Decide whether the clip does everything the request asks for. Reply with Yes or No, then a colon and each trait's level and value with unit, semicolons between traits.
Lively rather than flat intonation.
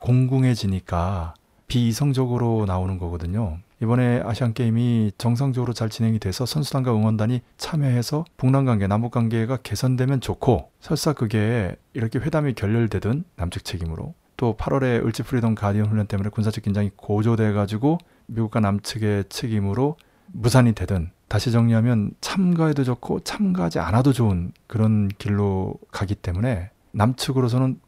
No: average, 3.7 semitones